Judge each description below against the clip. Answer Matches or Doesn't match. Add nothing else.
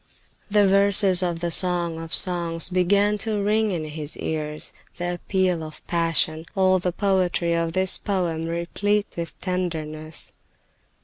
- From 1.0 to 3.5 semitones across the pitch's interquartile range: Matches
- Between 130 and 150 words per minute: Matches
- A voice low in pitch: Doesn't match